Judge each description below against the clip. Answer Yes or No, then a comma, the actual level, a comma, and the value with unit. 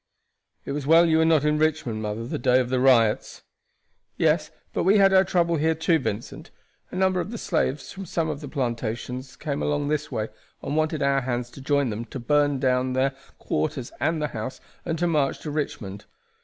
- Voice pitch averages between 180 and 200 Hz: No, medium, 145 Hz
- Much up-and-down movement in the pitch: No, average, 4.0 semitones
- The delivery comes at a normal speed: No, fast, 210 wpm